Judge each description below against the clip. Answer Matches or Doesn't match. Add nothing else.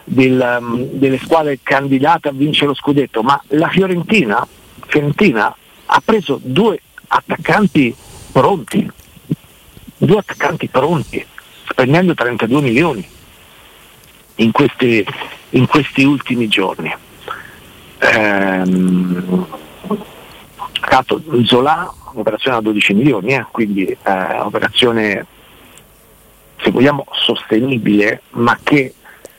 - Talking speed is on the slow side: Matches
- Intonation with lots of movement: Doesn't match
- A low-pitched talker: Matches